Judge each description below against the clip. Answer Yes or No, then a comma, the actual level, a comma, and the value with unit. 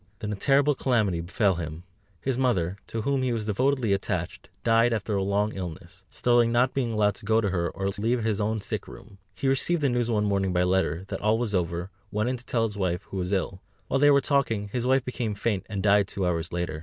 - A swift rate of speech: Yes, fast, 240 wpm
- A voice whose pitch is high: No, low, 105 Hz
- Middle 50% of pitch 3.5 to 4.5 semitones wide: Yes, average, 4.2 semitones